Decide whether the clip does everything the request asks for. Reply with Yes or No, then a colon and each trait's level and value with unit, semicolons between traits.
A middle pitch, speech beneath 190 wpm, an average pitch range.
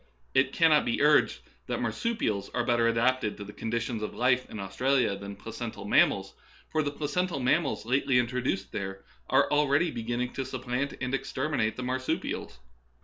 No: low, 125 Hz; average, 165 wpm; average, 3.5 semitones